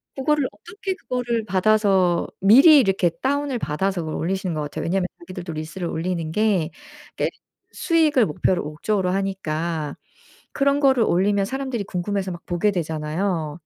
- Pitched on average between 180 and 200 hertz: Yes, high, 190 Hz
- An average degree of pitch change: No, wide, 5.7 semitones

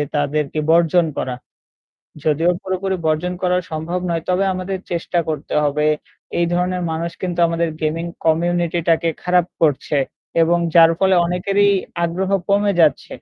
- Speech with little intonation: Yes, narrow, 2.2 semitones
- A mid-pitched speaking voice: Yes, medium, 170 Hz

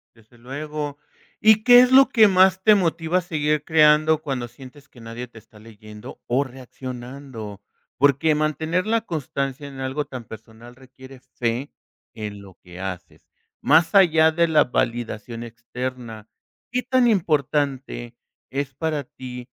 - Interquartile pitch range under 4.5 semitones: No, average, 4.8 semitones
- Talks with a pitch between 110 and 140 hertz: Yes, low, 135 Hz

